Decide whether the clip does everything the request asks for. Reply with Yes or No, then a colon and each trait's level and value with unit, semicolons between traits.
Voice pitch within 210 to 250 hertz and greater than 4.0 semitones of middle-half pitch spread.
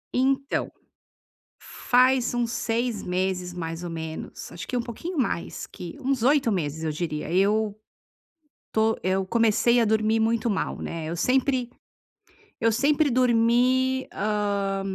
Yes: high, 225 Hz; average, 5.0 semitones